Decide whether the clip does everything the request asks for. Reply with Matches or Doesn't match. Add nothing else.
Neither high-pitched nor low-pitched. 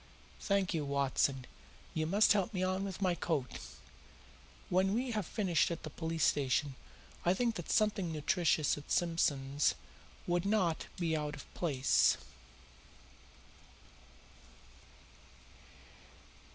Matches